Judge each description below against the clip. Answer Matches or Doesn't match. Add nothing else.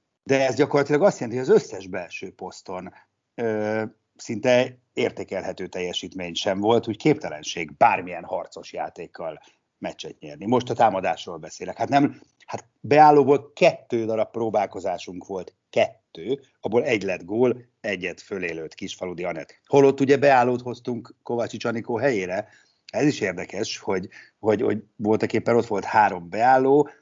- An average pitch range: Matches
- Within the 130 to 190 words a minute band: Matches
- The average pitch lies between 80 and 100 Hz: Doesn't match